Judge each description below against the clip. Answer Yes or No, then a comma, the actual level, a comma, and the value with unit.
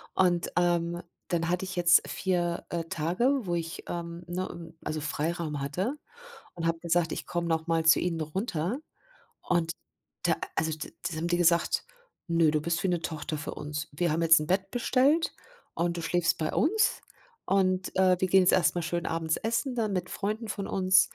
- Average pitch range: No, narrow, 2.3 semitones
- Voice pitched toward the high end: No, medium, 175 Hz